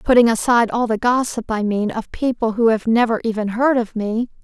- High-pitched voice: Yes, high, 230 Hz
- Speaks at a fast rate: Yes, fast, 215 wpm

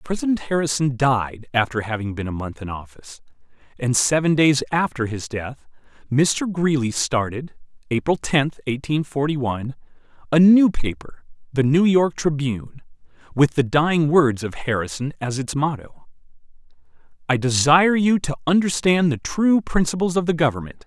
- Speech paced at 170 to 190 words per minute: No, average, 145 wpm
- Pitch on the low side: No, medium, 145 Hz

